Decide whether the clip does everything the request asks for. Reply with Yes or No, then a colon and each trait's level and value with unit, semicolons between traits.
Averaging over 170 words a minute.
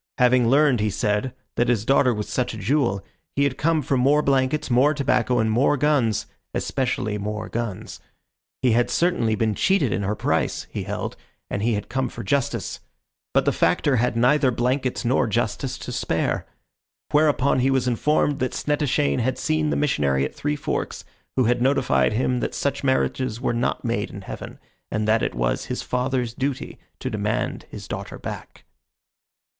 Yes: average, 180 wpm